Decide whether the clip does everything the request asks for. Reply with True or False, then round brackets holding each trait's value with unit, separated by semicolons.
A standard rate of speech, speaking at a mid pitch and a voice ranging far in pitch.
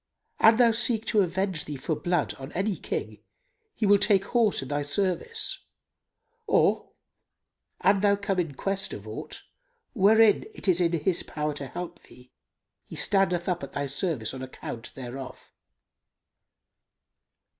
True (150 wpm; 180 Hz; 5.9 semitones)